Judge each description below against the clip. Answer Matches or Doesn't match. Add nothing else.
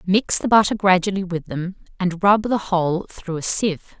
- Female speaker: Matches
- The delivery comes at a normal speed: Matches